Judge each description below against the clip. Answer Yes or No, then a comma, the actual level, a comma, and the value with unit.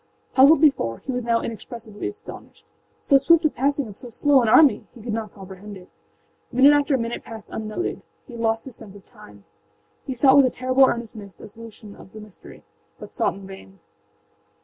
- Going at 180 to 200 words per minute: Yes, average, 195 wpm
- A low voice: No, high, 230 Hz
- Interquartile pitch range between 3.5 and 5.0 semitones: Yes, average, 4.3 semitones